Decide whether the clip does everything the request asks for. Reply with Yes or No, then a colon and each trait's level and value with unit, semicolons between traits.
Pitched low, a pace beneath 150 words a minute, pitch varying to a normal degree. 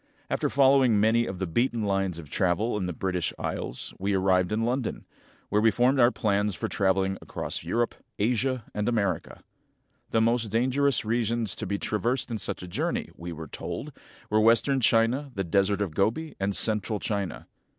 No: low, 105 Hz; average, 180 wpm; average, 3.5 semitones